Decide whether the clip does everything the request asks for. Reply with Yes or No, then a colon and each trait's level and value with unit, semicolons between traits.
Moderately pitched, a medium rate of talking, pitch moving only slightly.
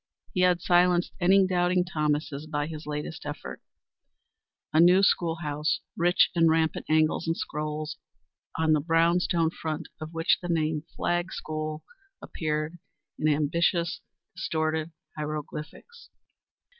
No: medium, 160 Hz; slow, 130 wpm; narrow, 2.2 semitones